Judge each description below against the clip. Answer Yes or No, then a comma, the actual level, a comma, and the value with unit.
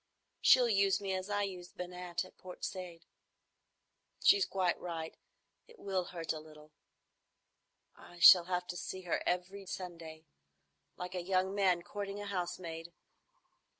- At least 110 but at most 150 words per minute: Yes, average, 140 wpm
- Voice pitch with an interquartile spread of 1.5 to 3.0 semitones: Yes, narrow, 2.4 semitones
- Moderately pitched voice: Yes, medium, 180 Hz